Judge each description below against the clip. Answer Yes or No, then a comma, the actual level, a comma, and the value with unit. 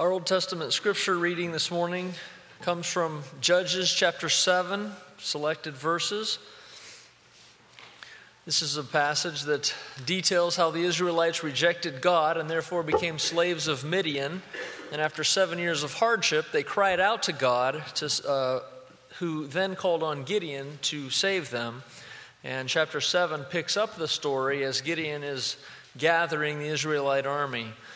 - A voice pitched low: No, medium, 165 Hz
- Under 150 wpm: Yes, average, 140 wpm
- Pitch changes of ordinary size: Yes, average, 3.5 semitones